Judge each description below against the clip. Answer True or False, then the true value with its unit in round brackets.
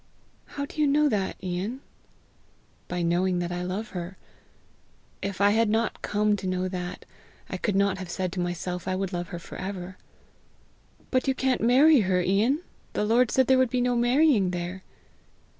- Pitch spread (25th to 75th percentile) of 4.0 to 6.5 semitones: True (5.2 semitones)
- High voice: True (195 Hz)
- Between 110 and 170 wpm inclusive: False (185 wpm)